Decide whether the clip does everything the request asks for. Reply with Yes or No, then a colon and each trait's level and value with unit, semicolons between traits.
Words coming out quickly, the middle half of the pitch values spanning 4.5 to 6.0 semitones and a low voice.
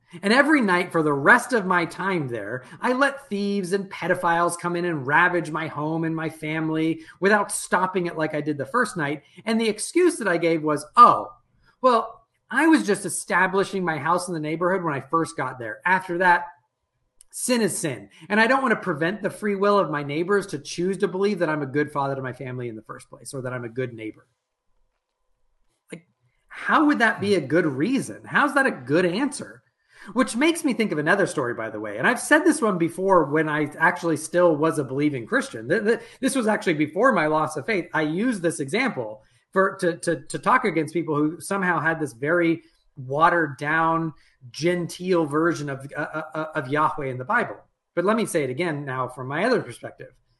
No: fast, 215 wpm; average, 4.9 semitones; medium, 170 Hz